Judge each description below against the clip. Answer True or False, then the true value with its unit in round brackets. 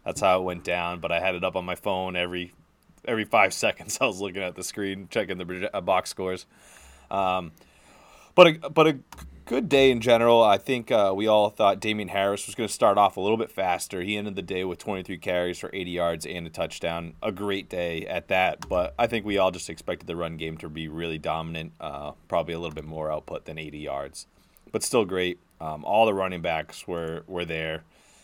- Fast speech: True (225 wpm)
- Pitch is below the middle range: True (90 Hz)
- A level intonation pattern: False (3.1 semitones)